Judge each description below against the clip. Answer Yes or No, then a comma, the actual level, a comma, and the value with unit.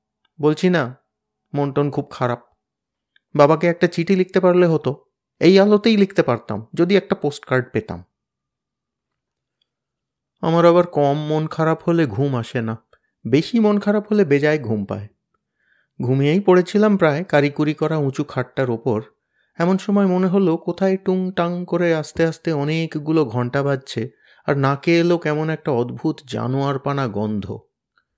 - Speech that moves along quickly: Yes, fast, 140 wpm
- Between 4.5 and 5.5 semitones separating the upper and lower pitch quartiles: Yes, average, 5.2 semitones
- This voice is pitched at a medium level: Yes, medium, 150 Hz